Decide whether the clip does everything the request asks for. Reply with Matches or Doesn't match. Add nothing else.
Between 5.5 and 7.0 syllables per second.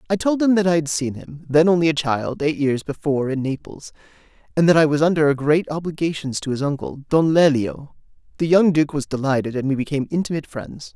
Matches